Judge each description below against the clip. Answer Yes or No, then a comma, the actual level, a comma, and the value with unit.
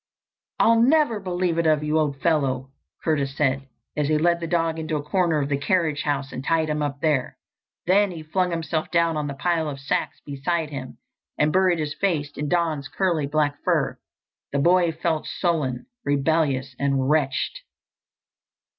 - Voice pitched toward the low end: No, medium, 155 Hz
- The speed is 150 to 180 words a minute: Yes, average, 175 wpm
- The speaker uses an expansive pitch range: No, average, 3.1 semitones